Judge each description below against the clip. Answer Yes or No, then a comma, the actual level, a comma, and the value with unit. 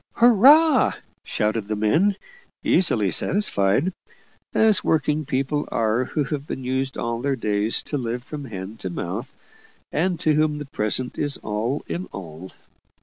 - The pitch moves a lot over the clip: Yes, wide, 6.3 semitones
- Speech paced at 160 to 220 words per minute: No, average, 145 wpm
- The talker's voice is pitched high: No, low, 135 Hz